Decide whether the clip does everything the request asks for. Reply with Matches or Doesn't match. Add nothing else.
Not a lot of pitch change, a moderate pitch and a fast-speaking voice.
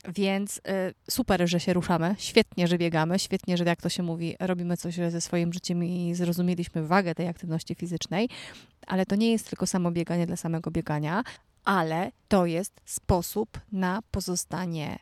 Matches